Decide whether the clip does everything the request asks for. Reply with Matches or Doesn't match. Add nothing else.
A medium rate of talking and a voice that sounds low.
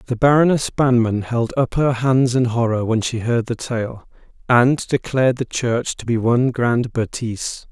Matches